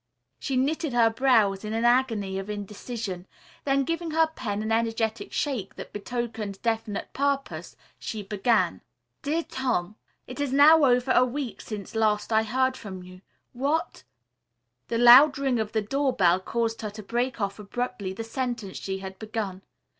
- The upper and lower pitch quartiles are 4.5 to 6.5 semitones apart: No, average, 4.1 semitones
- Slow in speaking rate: No, average, 165 wpm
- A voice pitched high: Yes, high, 230 Hz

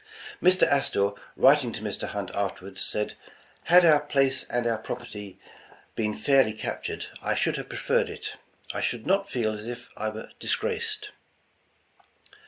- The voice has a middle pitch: No, low, 120 Hz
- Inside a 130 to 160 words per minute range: Yes, average, 150 wpm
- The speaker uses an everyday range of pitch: No, wide, 5.7 semitones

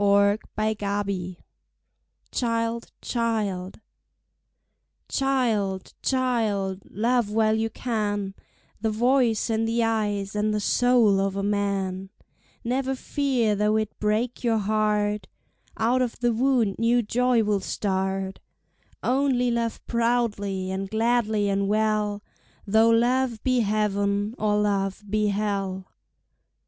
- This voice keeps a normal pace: No, slow, 110 wpm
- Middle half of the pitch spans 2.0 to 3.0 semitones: Yes, average, 2.7 semitones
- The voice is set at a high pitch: Yes, high, 215 Hz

